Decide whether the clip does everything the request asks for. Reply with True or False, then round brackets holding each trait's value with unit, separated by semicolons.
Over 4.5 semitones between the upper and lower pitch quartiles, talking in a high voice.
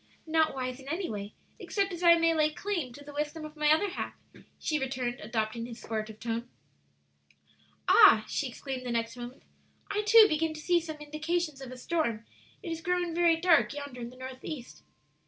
True (5.1 semitones; 295 Hz)